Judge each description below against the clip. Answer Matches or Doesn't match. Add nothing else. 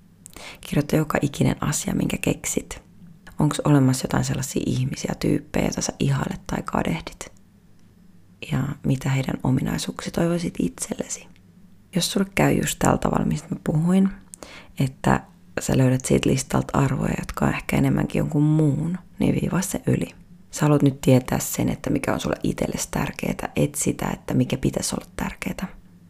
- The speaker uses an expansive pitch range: Matches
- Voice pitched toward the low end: Doesn't match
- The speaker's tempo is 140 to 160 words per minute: Matches